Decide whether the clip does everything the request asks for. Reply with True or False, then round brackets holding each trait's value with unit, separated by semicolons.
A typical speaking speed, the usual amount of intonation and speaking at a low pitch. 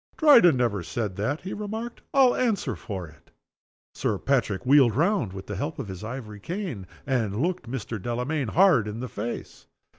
False (175 wpm; 8.8 semitones; 125 Hz)